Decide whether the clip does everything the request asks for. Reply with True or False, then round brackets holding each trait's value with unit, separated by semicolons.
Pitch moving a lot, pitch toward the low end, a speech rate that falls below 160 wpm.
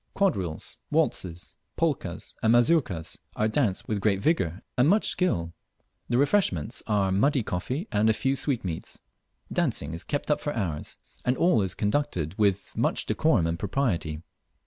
True (7.9 semitones; 105 Hz; 150 wpm)